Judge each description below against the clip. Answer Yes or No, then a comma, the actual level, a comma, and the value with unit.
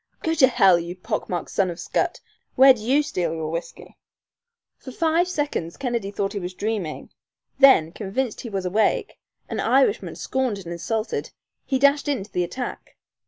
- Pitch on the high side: Yes, high, 215 Hz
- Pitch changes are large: Yes, wide, 6.8 semitones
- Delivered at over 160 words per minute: Yes, average, 180 wpm